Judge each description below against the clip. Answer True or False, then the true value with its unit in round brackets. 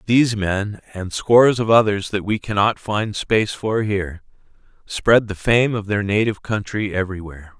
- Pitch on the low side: True (105 Hz)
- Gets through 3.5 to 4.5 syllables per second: False (5.1 syllables/s)